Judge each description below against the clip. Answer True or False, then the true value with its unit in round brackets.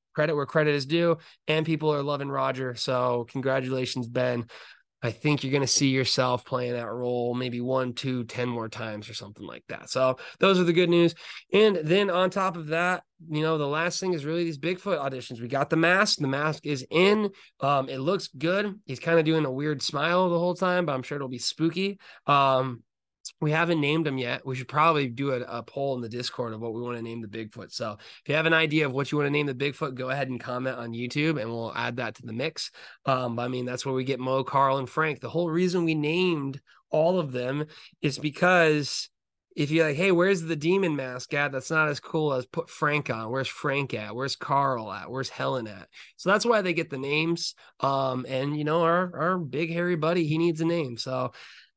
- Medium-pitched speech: True (145 Hz)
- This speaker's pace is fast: True (235 wpm)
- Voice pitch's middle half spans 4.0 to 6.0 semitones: True (4.4 semitones)